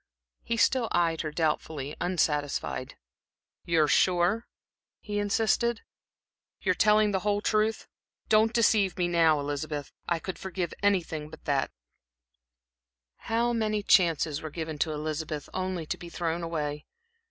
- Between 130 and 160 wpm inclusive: Yes, average, 140 wpm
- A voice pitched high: No, medium, 175 Hz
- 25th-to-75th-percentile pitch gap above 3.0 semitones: Yes, average, 4.9 semitones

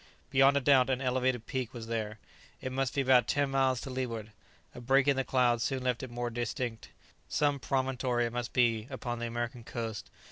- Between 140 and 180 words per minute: No, fast, 205 wpm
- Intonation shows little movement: Yes, narrow, 2.0 semitones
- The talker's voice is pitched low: Yes, low, 125 Hz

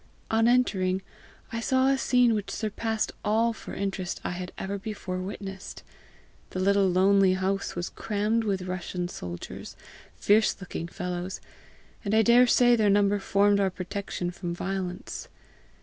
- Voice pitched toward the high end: Yes, high, 200 Hz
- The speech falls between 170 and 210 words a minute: No, average, 145 wpm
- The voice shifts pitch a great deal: No, average, 3.0 semitones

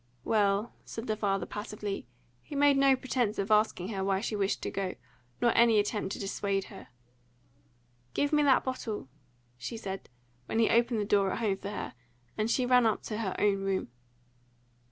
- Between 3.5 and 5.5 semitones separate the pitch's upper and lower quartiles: No, average, 3.0 semitones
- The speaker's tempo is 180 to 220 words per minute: Yes, average, 185 wpm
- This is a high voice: Yes, high, 210 Hz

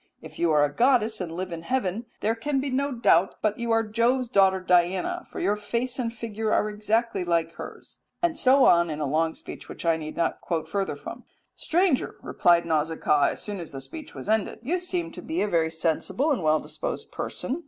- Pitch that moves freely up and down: Yes, wide, 6.9 semitones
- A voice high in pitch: Yes, high, 210 Hz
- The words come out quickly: Yes, fast, 215 wpm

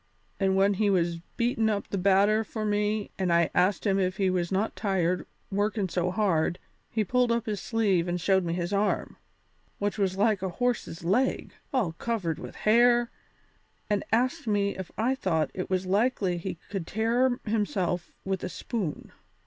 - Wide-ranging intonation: No, average, 3.2 semitones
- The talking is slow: No, average, 180 wpm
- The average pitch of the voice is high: Yes, high, 200 Hz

